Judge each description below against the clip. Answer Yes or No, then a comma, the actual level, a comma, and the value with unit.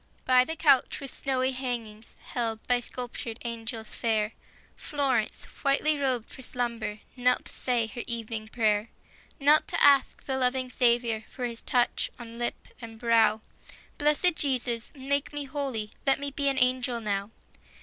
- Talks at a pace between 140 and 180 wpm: Yes, average, 160 wpm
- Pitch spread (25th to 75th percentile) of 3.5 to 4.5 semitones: No, average, 2.8 semitones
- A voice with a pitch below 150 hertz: No, high, 245 Hz